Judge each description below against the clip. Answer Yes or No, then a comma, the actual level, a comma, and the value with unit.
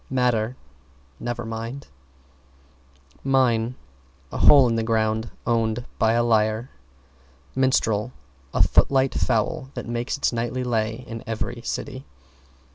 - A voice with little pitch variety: Yes, narrow, 2.1 semitones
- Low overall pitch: Yes, low, 115 Hz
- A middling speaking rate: No, slow, 120 wpm